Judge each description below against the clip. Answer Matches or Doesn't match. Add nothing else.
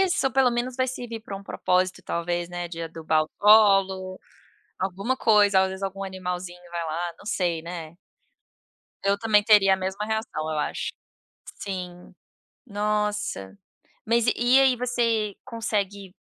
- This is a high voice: Matches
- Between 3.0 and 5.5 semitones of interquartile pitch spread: Matches